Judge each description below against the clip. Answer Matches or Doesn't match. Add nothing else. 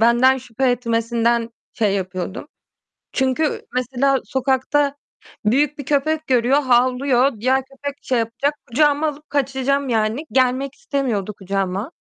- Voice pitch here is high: Matches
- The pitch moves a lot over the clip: Doesn't match